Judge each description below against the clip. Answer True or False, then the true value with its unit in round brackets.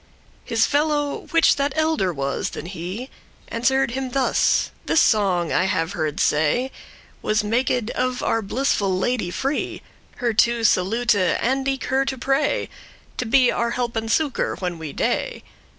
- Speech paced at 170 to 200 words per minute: False (155 wpm)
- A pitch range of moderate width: False (5.7 semitones)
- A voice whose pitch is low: False (235 Hz)